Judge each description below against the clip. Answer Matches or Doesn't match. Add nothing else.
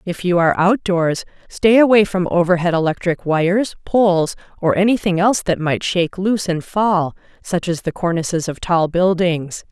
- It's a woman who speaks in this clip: Matches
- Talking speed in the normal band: Matches